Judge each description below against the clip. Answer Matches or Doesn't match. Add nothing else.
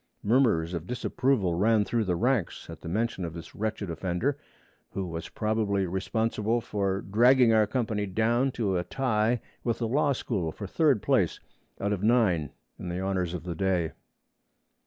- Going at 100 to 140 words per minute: Doesn't match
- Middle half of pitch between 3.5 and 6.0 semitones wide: Matches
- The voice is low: Matches